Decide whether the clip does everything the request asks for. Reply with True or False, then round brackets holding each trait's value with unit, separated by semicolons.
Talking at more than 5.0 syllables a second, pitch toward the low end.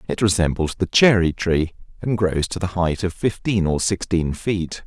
False (4.6 syllables/s; 90 Hz)